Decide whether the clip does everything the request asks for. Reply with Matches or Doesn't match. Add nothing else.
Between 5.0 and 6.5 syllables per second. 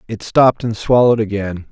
Matches